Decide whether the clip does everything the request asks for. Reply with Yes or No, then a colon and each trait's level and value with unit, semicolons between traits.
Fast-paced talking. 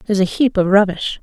Yes: fast, 245 wpm